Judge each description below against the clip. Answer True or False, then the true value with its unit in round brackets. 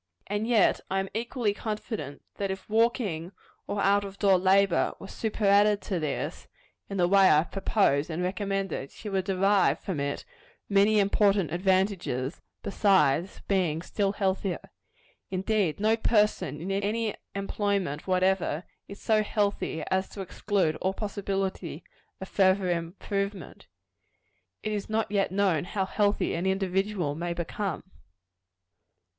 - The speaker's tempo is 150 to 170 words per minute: False (140 wpm)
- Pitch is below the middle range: False (195 Hz)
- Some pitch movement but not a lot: False (2.0 semitones)